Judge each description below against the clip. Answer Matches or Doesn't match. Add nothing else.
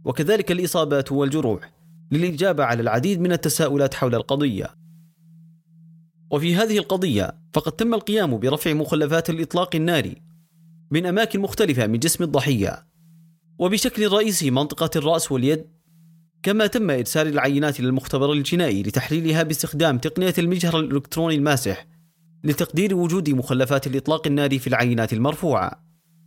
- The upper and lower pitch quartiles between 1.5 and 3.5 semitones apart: Matches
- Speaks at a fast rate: Doesn't match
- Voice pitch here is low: Doesn't match